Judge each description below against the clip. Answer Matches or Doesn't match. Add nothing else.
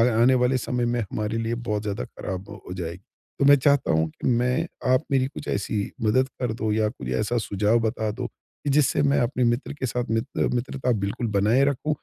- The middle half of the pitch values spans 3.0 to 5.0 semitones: Matches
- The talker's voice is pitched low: Matches